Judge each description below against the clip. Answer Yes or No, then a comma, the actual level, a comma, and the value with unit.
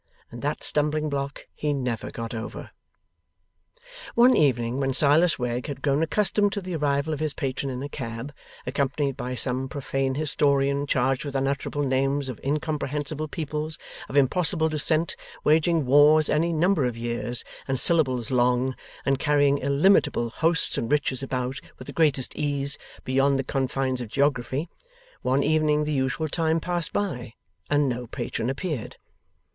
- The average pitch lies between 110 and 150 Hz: Yes, medium, 140 Hz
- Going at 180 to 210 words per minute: No, average, 155 wpm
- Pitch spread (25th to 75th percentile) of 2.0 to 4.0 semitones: Yes, average, 2.8 semitones